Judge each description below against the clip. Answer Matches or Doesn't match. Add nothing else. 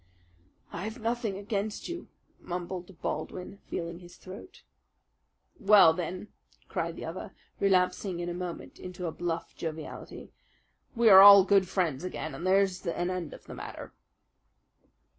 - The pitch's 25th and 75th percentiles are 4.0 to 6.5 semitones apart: Doesn't match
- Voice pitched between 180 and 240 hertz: Matches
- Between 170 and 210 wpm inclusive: Doesn't match